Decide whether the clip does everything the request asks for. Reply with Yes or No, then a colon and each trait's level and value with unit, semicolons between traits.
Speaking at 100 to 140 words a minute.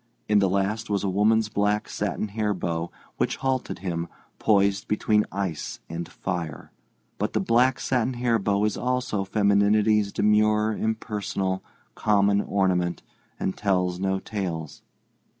Yes: slow, 135 wpm